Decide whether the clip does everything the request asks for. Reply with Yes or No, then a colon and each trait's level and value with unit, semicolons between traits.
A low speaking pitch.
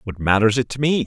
Yes: low, 120 Hz